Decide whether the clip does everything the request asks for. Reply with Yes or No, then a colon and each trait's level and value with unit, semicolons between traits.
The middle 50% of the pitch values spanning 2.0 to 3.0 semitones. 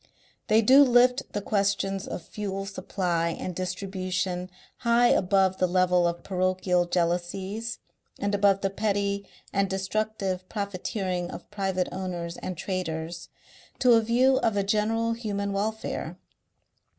Yes: narrow, 2.4 semitones